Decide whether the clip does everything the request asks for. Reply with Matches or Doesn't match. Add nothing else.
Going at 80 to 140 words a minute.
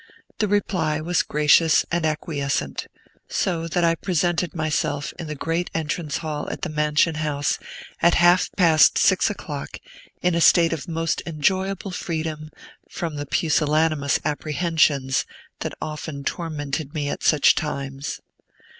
Matches